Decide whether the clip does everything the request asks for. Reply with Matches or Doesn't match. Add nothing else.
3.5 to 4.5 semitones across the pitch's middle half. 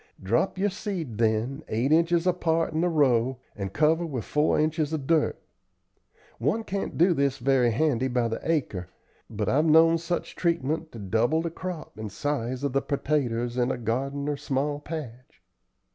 Doesn't match